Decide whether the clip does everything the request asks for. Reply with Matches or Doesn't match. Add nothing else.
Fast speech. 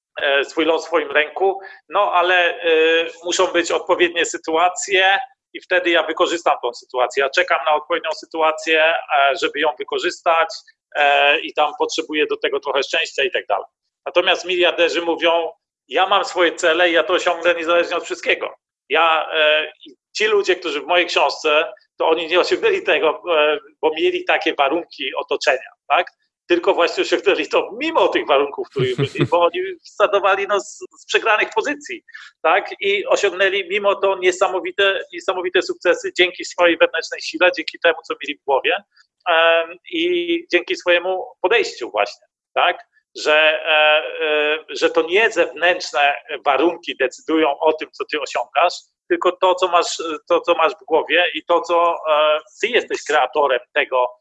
Doesn't match